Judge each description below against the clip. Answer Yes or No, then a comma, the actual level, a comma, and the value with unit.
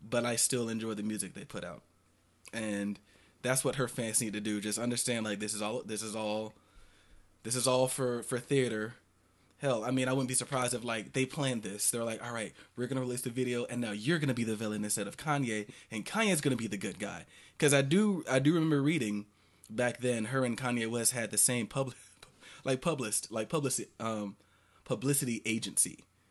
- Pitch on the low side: Yes, low, 115 Hz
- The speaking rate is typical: No, fast, 210 wpm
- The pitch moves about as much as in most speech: Yes, average, 3.3 semitones